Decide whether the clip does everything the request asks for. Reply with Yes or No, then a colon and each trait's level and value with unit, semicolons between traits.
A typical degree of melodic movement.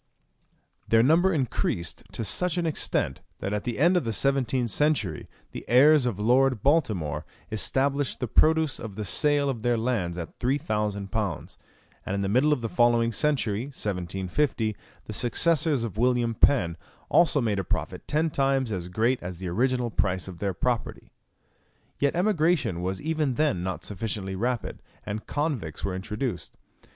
No: wide, 6.1 semitones